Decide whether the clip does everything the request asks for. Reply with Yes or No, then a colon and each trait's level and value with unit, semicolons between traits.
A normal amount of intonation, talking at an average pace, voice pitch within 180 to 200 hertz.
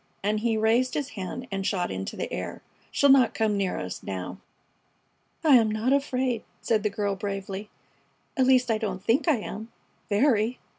No: average, 4.3 semitones; average, 180 wpm; high, 220 Hz